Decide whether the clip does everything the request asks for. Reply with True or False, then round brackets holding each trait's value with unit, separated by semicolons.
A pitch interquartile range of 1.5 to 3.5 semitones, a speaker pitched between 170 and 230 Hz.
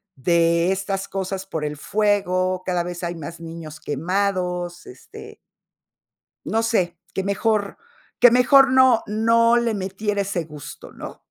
False (3.9 semitones; 190 Hz)